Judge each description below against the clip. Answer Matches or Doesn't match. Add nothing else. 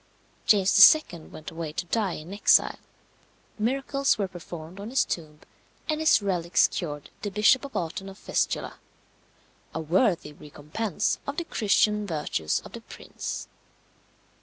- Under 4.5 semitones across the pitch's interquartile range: Doesn't match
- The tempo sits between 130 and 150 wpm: Matches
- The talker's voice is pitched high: Matches